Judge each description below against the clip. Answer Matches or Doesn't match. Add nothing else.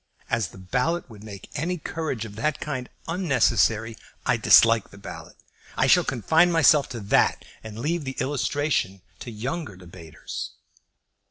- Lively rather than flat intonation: Matches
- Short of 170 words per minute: Matches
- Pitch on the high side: Doesn't match